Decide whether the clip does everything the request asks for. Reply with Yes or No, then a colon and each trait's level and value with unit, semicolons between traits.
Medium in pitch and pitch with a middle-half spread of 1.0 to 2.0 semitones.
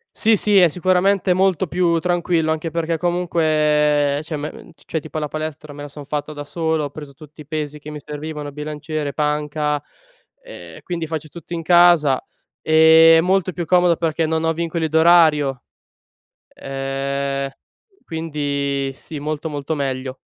No: medium, 155 Hz; narrow, 2.4 semitones